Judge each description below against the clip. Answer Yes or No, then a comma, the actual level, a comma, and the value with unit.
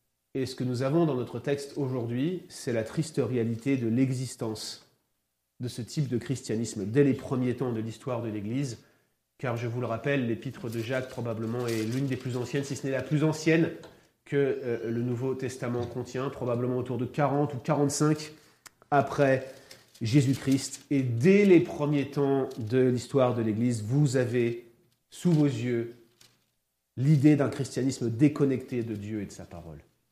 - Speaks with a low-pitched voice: Yes, low, 130 Hz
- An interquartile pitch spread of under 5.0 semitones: Yes, average, 3.0 semitones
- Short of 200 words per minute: Yes, average, 170 wpm